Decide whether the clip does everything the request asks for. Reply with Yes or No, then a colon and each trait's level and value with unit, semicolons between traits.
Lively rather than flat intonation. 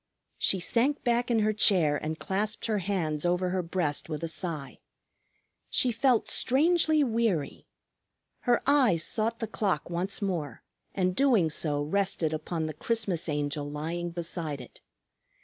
Yes: wide, 6.1 semitones